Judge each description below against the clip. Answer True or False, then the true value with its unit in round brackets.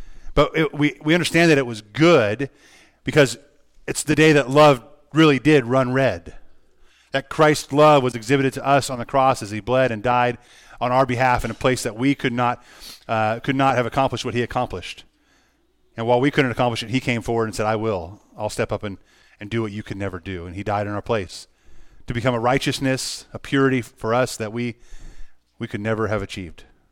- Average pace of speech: False (215 wpm)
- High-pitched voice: False (125 Hz)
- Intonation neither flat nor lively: True (3.6 semitones)